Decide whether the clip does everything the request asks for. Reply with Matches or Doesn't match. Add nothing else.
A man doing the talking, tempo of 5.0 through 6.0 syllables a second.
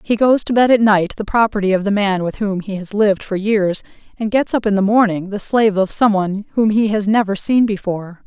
Doesn't match